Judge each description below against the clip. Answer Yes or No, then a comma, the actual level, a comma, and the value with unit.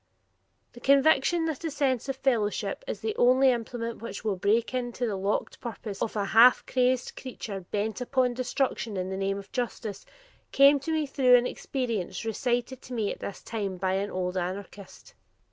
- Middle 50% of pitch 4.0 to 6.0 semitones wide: Yes, average, 4.4 semitones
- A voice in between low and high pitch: No, high, 240 Hz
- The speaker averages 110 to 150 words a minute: No, average, 180 wpm